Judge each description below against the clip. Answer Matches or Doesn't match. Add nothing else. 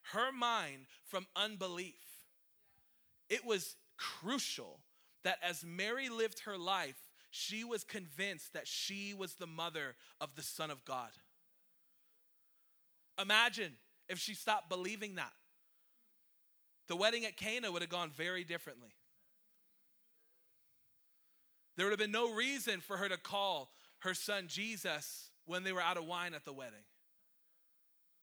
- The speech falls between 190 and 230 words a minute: Doesn't match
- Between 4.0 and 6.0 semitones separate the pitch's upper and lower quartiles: Doesn't match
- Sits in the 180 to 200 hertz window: Matches